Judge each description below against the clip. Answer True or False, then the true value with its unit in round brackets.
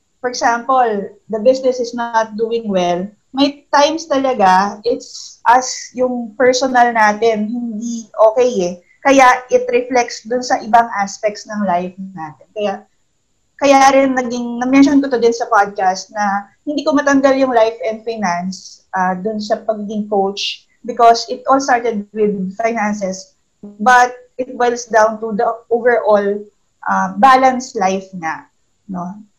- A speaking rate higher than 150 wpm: False (145 wpm)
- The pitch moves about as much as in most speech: True (3.5 semitones)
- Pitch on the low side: False (230 Hz)